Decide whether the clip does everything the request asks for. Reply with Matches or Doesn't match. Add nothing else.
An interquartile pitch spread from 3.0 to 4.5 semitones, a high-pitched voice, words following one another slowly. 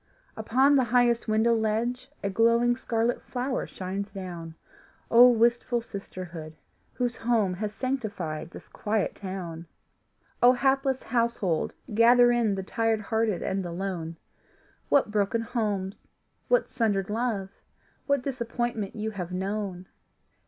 Matches